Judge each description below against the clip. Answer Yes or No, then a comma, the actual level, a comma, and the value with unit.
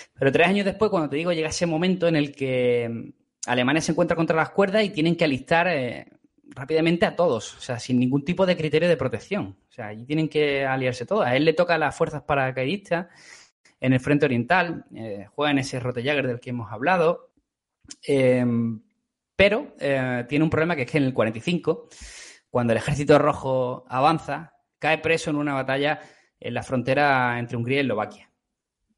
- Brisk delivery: Yes, fast, 195 wpm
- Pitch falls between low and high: Yes, medium, 150 Hz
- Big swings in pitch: No, average, 4.6 semitones